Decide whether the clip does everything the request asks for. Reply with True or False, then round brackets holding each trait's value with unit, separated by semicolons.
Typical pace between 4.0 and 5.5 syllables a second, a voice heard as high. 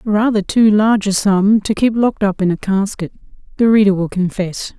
True (5.2 syllables/s; 205 Hz)